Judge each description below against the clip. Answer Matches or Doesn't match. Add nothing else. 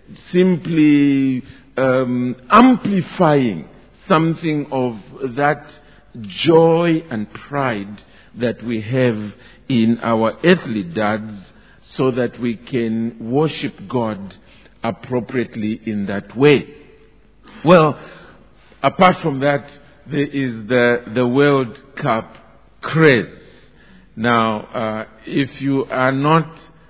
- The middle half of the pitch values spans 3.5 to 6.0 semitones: Matches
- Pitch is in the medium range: Doesn't match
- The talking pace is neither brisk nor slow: Doesn't match